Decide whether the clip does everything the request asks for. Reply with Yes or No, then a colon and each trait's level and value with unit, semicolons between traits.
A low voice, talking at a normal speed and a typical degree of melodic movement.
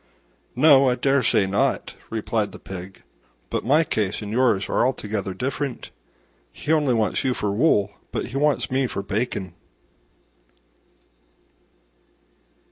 No: low, 120 Hz; slow, 130 wpm; average, 4.8 semitones